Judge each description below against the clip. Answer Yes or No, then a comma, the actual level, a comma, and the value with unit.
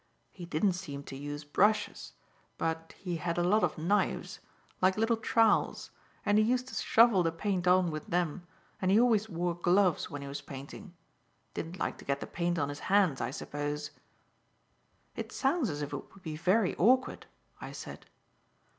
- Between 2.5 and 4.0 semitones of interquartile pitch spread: No, average, 5.1 semitones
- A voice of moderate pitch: Yes, medium, 180 Hz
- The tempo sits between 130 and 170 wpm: No, average, 180 wpm